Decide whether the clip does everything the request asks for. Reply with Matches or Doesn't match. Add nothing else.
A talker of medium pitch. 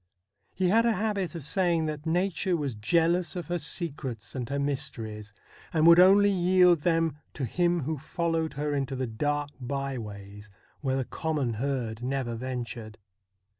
Matches